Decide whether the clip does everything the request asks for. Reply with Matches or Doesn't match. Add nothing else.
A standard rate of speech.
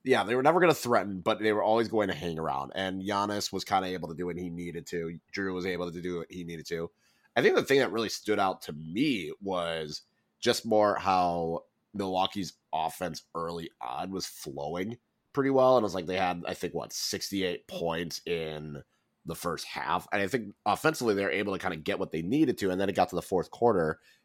Doesn't match